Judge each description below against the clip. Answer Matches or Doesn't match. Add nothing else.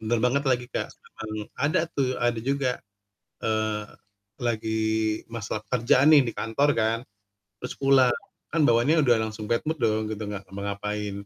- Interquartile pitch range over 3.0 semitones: Matches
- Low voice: Matches